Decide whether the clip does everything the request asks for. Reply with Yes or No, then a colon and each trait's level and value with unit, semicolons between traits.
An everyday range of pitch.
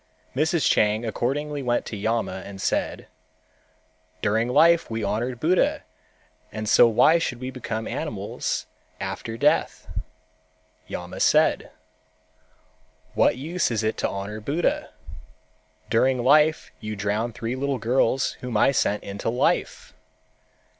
Yes: average, 3.9 semitones